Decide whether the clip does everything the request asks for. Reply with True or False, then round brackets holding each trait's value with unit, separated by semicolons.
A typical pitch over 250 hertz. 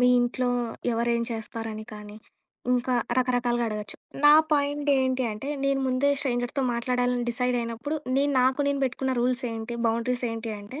False (245 Hz)